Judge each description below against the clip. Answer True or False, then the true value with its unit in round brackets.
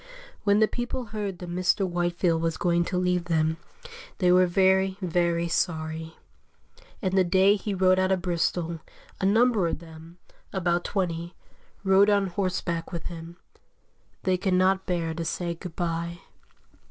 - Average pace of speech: True (155 wpm)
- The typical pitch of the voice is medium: True (180 Hz)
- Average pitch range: False (2.1 semitones)